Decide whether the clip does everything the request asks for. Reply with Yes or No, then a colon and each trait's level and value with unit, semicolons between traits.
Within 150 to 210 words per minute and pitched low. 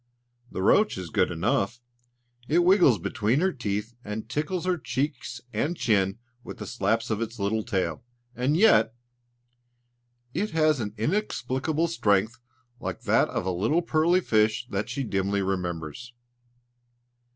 No: average, 140 wpm; low, 115 Hz